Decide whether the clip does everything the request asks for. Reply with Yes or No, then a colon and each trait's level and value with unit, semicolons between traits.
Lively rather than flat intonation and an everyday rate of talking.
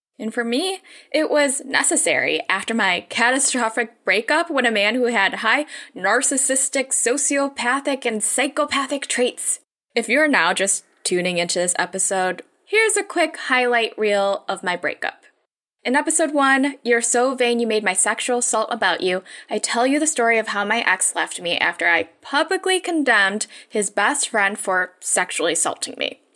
Yes: wide, 5.7 semitones; average, 165 wpm